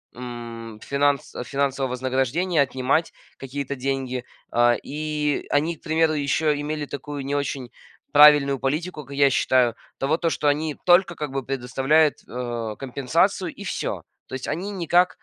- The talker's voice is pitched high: No, medium, 140 Hz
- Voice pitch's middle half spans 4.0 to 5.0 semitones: No, average, 3.0 semitones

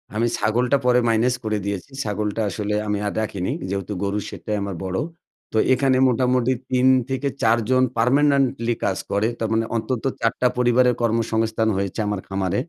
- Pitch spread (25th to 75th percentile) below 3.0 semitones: No, average, 3.3 semitones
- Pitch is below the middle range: Yes, low, 115 Hz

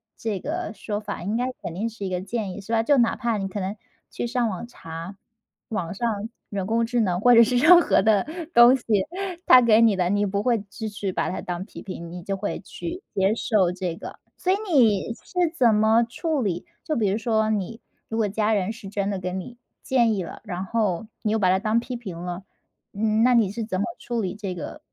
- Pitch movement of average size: Yes, average, 3.4 semitones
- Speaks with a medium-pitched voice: No, high, 215 Hz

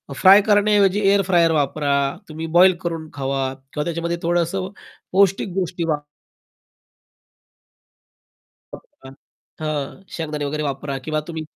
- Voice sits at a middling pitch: Yes, medium, 165 Hz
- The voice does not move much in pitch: No, average, 4.0 semitones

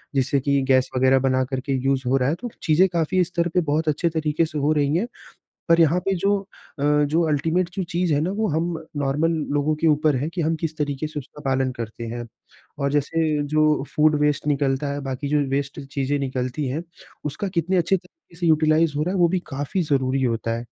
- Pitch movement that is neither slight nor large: Yes, average, 3.4 semitones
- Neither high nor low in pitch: Yes, medium, 150 Hz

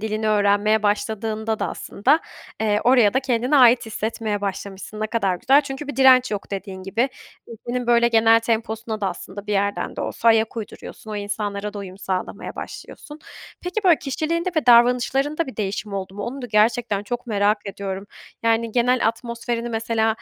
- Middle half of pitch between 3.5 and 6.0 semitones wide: No, average, 3.0 semitones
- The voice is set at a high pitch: Yes, high, 220 Hz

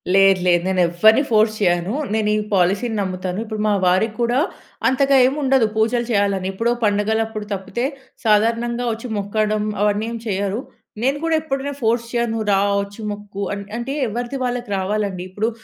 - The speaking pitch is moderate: No, high, 215 Hz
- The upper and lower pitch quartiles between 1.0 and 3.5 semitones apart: Yes, average, 3.0 semitones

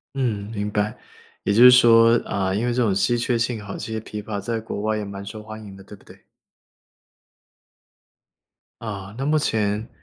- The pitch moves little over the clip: Yes, narrow, 2.2 semitones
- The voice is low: Yes, low, 110 Hz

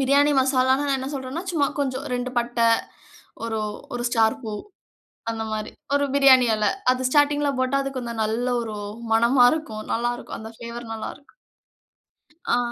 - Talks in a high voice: Yes, very high, 255 Hz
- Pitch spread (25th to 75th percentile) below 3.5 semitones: Yes, average, 3.1 semitones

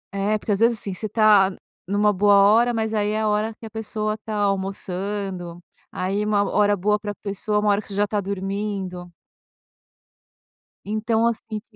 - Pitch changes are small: Yes, narrow, 1.4 semitones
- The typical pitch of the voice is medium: No, high, 205 Hz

